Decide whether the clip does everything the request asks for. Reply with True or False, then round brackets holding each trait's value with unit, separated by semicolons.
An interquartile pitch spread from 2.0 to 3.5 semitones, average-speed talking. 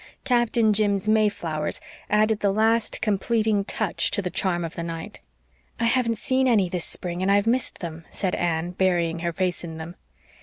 False (4.1 semitones; 180 wpm)